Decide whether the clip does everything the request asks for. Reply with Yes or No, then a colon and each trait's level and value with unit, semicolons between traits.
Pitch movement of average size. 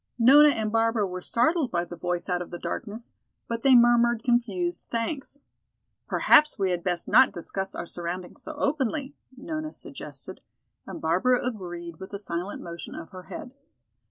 No: wide, 6.0 semitones